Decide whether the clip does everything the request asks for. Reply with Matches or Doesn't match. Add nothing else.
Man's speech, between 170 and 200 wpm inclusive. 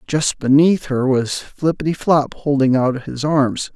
Doesn't match